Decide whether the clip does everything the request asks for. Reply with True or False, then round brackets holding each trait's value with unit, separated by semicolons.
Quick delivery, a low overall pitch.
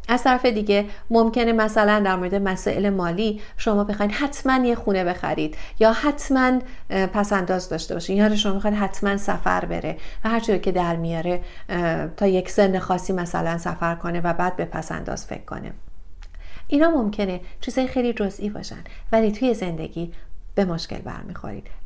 False (160 wpm; 200 Hz)